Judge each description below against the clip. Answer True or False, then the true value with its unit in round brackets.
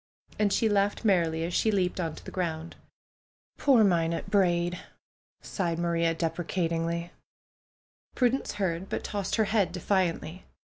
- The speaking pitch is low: False (180 Hz)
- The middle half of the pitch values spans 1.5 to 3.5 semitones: True (3.2 semitones)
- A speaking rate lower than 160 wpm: True (145 wpm)